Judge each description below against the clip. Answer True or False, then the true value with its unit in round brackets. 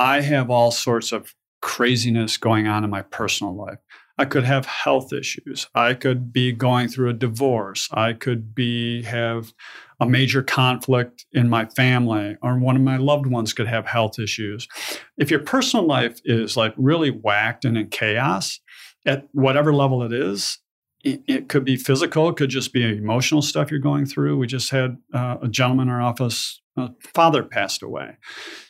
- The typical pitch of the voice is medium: False (125 Hz)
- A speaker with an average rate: True (185 wpm)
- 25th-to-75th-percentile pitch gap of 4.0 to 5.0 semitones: False (2.6 semitones)